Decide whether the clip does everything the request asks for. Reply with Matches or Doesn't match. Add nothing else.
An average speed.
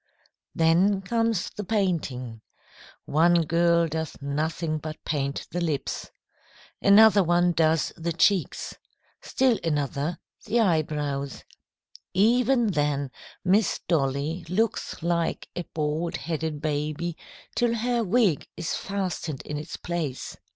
Doesn't match